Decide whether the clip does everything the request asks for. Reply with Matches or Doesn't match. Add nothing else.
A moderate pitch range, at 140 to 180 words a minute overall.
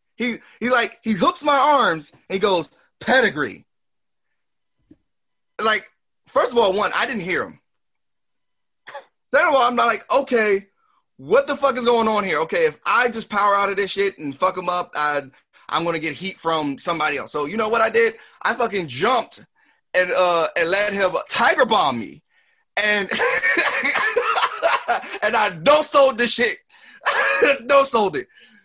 Doesn't match